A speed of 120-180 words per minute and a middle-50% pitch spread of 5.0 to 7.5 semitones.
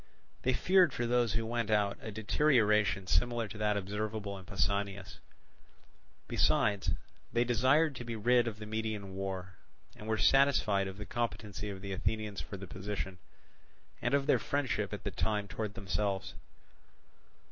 No: average, 160 wpm; average, 3.0 semitones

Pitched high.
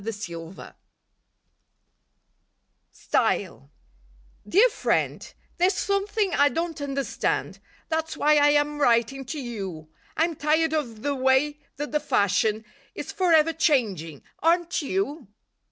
Yes: very high, 290 Hz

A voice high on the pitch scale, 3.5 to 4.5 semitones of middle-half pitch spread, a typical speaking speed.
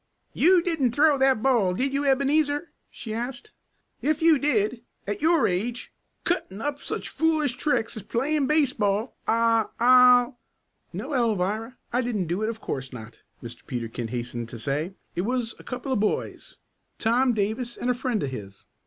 No: high, 240 Hz; wide, 5.4 semitones; average, 170 wpm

